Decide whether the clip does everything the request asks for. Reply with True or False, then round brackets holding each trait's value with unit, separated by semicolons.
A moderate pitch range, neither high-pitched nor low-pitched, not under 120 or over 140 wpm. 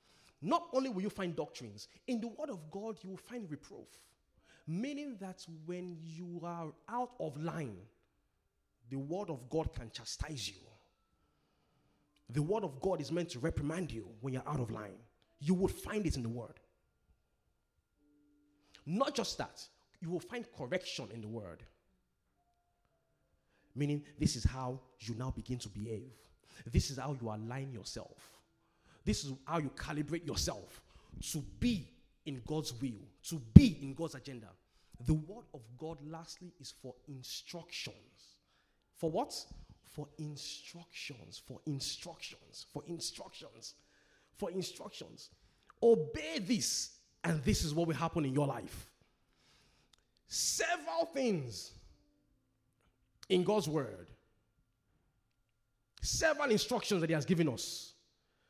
False (6.7 semitones; 145 Hz; 135 wpm)